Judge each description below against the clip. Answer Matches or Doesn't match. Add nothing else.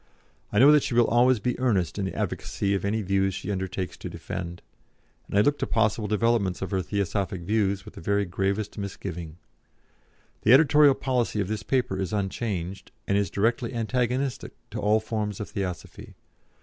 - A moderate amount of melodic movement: Matches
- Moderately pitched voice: Doesn't match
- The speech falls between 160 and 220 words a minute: Matches